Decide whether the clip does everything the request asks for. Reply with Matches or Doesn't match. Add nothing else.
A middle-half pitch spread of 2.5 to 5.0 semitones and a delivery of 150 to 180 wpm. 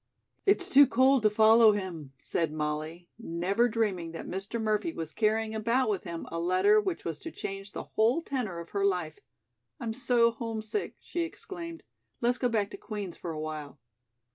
Doesn't match